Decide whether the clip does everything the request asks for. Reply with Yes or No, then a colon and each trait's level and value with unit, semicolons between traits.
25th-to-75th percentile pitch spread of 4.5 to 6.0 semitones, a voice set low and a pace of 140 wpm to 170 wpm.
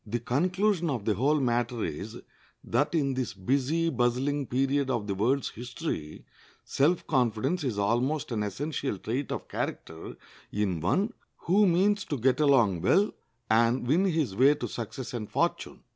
Yes: average, 5.2 semitones; low, 130 Hz; average, 160 wpm